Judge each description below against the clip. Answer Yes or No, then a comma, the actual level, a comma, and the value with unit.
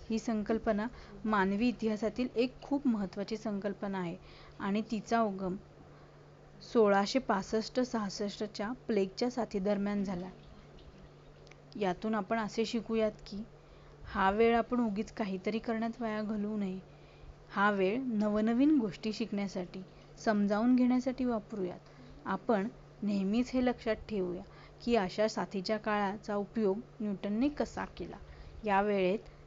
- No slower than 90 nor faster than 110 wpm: Yes, average, 100 wpm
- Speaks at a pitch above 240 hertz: No, high, 215 Hz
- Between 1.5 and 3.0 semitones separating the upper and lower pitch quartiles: Yes, narrow, 2.4 semitones